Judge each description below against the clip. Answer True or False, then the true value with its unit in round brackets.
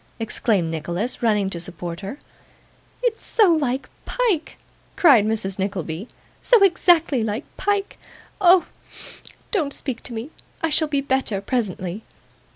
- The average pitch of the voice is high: True (240 Hz)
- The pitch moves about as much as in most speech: False (8.8 semitones)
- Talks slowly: True (130 wpm)